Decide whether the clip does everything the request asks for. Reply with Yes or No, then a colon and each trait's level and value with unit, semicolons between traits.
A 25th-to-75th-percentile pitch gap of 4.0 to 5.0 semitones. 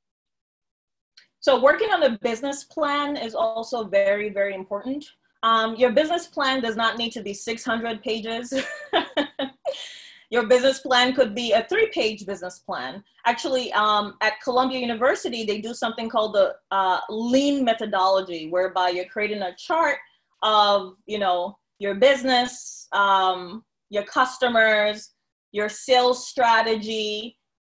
Yes: average, 4.3 semitones